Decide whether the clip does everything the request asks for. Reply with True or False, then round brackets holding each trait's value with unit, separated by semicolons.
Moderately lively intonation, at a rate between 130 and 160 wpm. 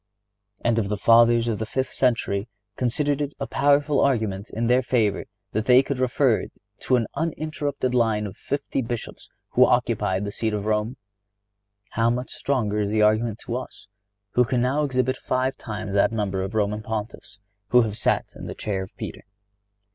False (3.3 semitones; 185 wpm)